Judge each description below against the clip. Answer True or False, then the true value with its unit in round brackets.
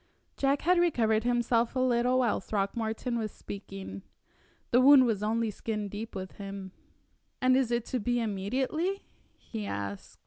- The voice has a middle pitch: False (230 Hz)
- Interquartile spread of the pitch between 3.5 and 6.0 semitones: True (3.8 semitones)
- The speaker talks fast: False (150 wpm)